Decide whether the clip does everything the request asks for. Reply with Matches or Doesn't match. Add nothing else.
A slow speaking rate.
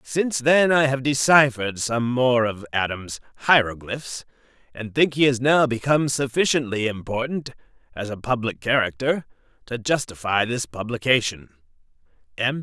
Matches